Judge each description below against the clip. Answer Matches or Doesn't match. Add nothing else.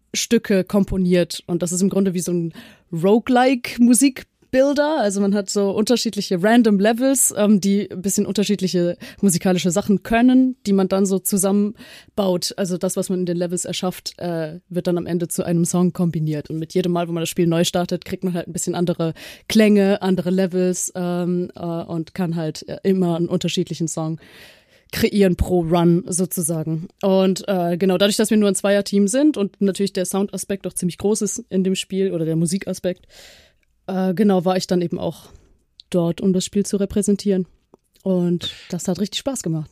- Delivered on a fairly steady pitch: Matches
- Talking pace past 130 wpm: Matches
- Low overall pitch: Doesn't match